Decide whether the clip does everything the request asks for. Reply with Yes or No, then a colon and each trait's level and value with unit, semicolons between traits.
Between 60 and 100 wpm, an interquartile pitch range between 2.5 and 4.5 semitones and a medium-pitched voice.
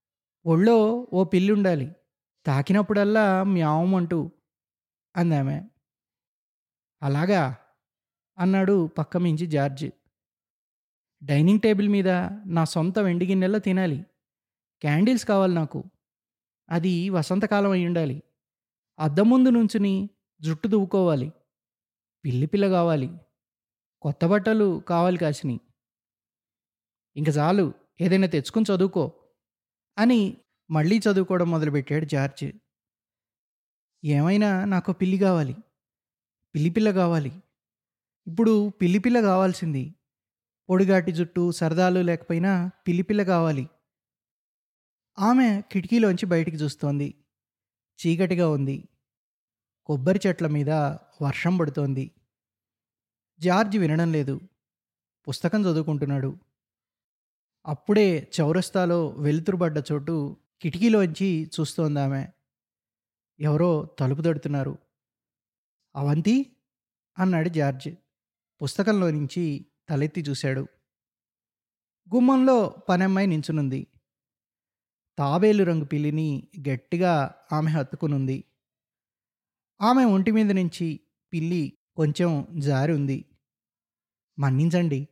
No: average, 80 wpm; average, 4.9 semitones; medium, 165 Hz